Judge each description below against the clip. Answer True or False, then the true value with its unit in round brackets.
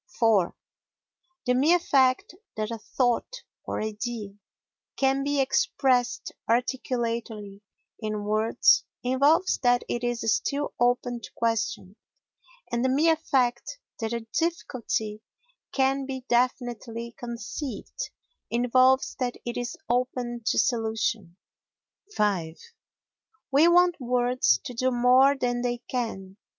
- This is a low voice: False (245 Hz)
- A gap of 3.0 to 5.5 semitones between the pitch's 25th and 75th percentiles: False (2.6 semitones)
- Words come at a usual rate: False (115 wpm)